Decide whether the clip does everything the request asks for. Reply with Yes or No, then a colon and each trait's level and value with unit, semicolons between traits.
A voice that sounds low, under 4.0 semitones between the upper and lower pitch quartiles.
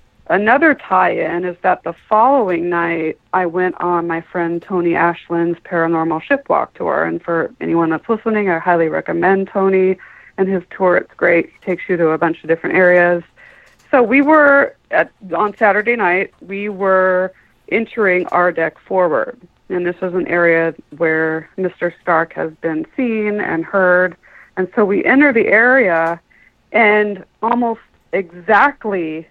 No: medium, 180 Hz; average, 3.3 semitones